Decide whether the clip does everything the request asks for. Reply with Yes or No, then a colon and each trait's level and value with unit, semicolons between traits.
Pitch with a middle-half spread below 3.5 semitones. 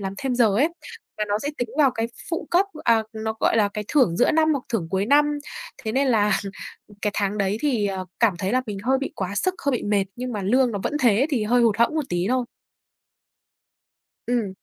No: average, 4.4 semitones